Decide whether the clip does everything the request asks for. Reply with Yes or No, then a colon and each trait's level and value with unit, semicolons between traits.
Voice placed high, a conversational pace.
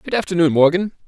No: medium, 180 Hz; average, 170 wpm